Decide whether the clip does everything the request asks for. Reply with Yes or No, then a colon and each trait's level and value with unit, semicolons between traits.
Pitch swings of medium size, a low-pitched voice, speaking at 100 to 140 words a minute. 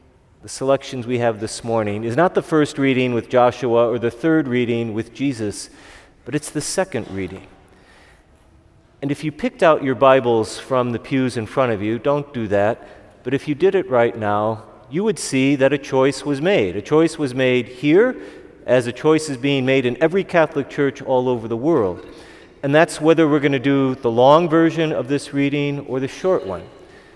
No: average, 4.2 semitones; low, 130 Hz; fast, 205 wpm